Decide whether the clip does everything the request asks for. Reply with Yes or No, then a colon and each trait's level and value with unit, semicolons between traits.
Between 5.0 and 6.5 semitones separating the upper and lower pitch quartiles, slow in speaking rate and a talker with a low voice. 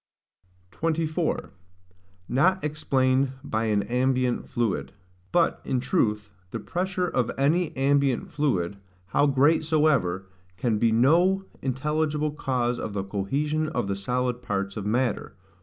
Yes: wide, 5.4 semitones; slow, 125 wpm; low, 130 Hz